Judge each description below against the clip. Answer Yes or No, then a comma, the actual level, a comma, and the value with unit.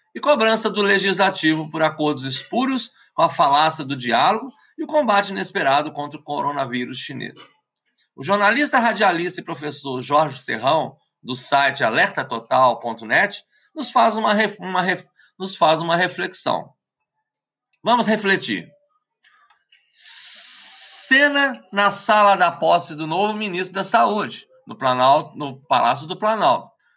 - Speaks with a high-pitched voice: Yes, high, 195 Hz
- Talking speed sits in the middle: Yes, average, 130 wpm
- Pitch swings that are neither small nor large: No, wide, 7.7 semitones